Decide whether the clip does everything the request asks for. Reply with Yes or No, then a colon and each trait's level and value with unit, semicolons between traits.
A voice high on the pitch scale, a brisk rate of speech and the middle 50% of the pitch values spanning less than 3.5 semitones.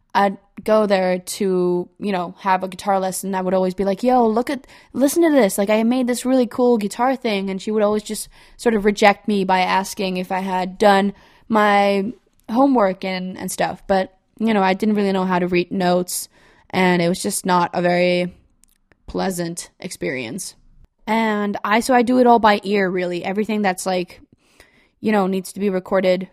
Yes: high, 200 Hz; fast, 200 wpm; narrow, 2.6 semitones